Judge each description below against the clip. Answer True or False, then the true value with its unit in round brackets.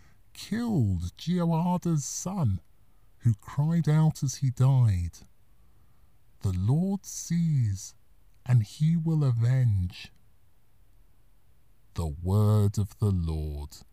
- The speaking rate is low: True (90 wpm)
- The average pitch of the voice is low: True (110 Hz)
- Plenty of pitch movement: True (6.7 semitones)